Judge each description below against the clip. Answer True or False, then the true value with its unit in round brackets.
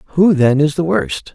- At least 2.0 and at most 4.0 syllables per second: True (3.8 syllables/s)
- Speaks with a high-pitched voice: False (160 Hz)